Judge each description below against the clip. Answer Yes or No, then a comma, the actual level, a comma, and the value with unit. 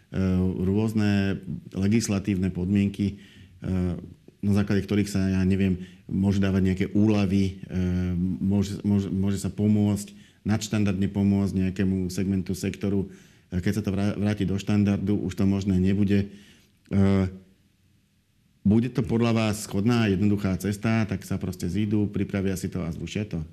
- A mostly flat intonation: Yes, narrow, 1.3 semitones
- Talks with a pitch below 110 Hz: Yes, low, 100 Hz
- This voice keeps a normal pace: Yes, average, 130 wpm